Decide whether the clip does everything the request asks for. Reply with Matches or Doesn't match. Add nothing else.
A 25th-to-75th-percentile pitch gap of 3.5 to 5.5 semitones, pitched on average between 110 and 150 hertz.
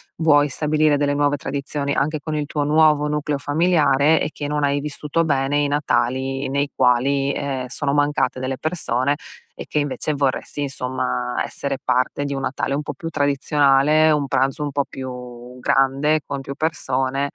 Doesn't match